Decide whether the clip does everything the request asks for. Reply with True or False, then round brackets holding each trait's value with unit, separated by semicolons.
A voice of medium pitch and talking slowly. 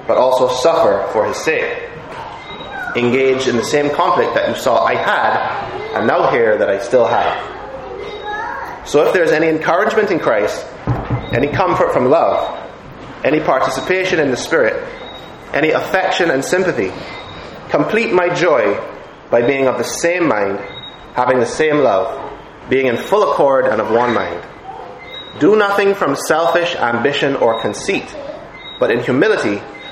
False (175 Hz; 150 wpm)